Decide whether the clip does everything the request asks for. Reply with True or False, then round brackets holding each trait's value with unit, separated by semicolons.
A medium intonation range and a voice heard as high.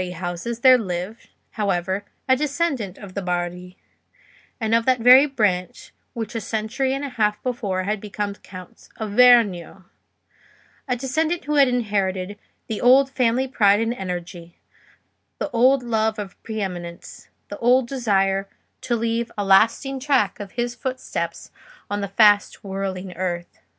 True (4.5 semitones; 215 Hz)